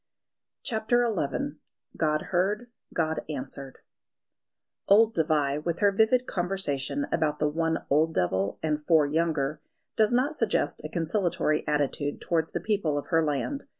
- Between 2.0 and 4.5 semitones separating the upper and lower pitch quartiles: No, wide, 5.5 semitones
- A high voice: No, medium, 160 Hz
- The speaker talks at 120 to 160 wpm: Yes, average, 140 wpm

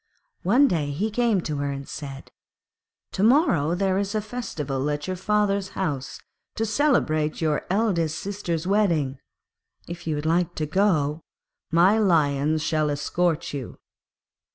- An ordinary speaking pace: Yes, average, 145 wpm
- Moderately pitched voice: Yes, medium, 170 Hz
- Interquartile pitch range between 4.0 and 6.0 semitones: Yes, average, 5.2 semitones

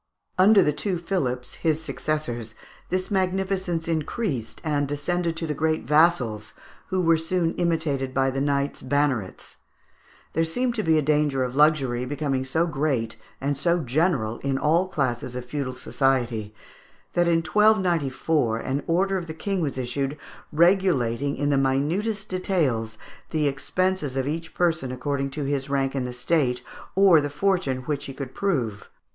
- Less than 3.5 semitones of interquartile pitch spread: No, average, 4.4 semitones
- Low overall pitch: No, medium, 150 Hz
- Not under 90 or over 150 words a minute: No, average, 160 wpm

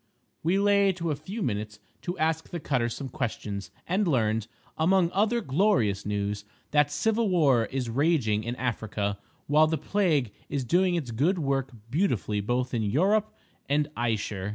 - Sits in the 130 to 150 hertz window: Yes, medium, 140 Hz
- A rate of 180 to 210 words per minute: No, average, 160 wpm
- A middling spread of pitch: No, wide, 7.8 semitones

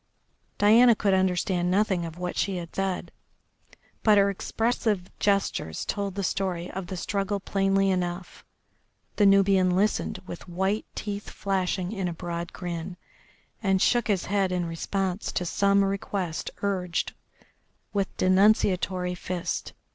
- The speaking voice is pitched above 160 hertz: Yes, high, 190 Hz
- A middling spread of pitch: No, narrow, 1.9 semitones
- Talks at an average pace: No, slow, 130 wpm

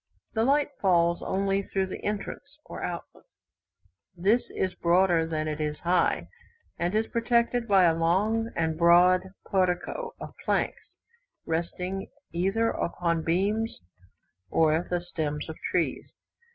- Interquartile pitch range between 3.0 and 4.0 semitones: Yes, average, 3.7 semitones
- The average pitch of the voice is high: No, medium, 180 Hz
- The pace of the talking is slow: Yes, slow, 130 wpm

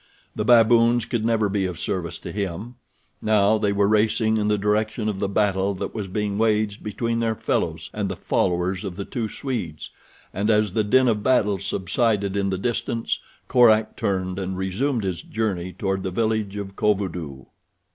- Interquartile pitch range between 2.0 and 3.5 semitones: Yes, narrow, 2.5 semitones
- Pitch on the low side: Yes, low, 105 Hz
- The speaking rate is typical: Yes, average, 180 wpm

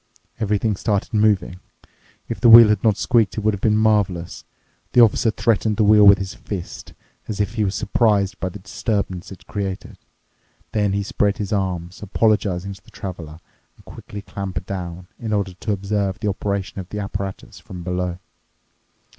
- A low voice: Yes, low, 100 Hz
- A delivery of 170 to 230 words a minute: Yes, average, 175 wpm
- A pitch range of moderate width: No, narrow, 2.1 semitones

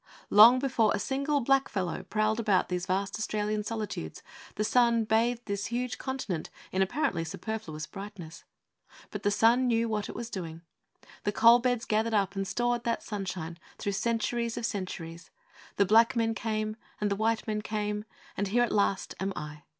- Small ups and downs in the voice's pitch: No, average, 3.0 semitones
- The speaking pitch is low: No, high, 215 Hz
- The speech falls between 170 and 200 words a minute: Yes, average, 175 wpm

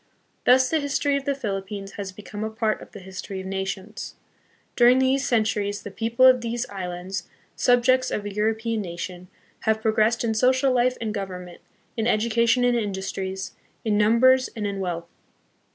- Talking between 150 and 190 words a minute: Yes, average, 175 wpm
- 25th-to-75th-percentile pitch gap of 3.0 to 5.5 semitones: Yes, average, 3.9 semitones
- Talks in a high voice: Yes, high, 220 Hz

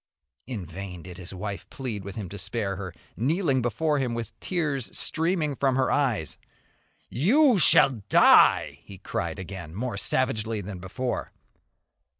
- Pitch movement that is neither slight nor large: No, wide, 6.1 semitones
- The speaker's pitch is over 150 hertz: No, low, 115 Hz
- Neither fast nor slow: Yes, average, 150 wpm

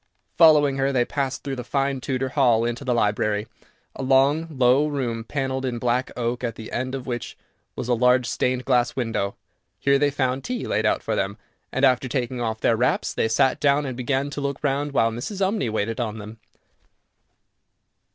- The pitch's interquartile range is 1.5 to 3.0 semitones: Yes, narrow, 2.6 semitones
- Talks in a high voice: No, low, 130 Hz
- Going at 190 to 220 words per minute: Yes, average, 195 wpm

